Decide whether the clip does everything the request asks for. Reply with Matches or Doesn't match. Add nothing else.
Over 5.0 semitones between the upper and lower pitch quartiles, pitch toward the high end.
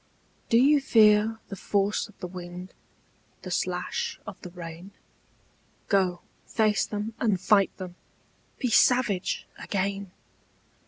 Doesn't match